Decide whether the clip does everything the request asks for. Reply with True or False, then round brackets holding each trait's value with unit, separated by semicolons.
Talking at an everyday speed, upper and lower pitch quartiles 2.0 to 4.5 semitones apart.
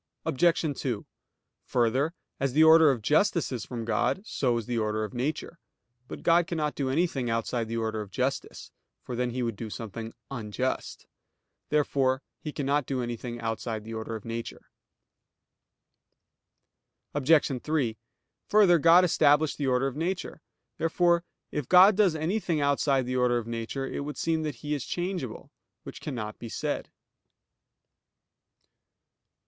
False (150 wpm; 5.2 semitones)